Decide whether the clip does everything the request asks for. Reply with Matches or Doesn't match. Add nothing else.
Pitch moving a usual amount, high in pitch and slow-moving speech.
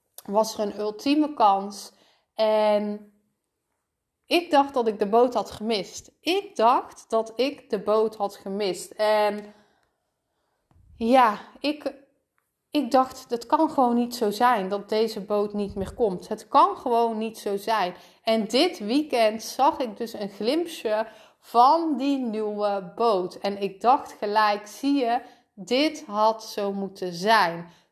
Doesn't match